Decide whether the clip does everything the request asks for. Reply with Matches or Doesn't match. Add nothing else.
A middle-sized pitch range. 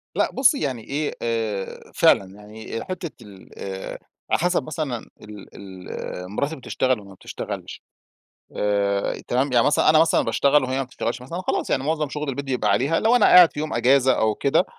Doesn't match